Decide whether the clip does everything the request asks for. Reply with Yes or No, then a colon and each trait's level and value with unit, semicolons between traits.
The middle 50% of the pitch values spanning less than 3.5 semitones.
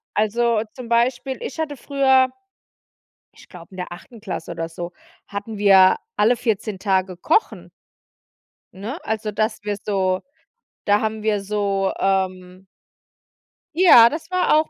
No: average, 3.9 semitones